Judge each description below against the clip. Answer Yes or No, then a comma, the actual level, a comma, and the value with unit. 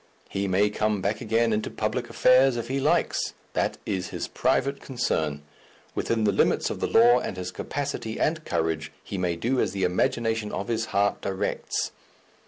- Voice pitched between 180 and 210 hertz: No, low, 110 Hz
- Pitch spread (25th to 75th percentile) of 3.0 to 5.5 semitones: Yes, average, 4.2 semitones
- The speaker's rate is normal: Yes, average, 180 wpm